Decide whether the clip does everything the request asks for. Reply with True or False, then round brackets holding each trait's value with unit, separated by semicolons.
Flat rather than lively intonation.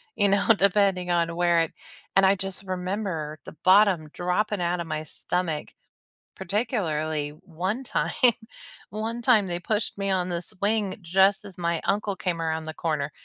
False (3.2 semitones)